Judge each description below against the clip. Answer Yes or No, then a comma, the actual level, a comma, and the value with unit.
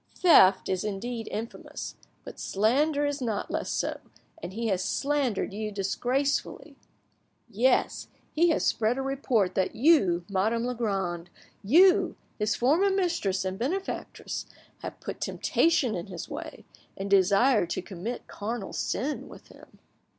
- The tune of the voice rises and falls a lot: Yes, wide, 6.1 semitones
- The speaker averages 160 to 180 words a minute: No, slow, 135 wpm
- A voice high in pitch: Yes, high, 225 Hz